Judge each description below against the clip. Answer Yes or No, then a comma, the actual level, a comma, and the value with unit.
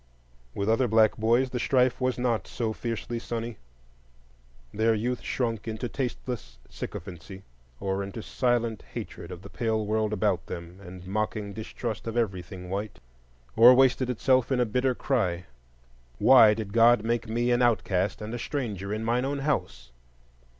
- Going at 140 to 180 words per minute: Yes, average, 155 wpm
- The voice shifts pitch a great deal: No, average, 3.3 semitones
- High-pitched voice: No, low, 115 Hz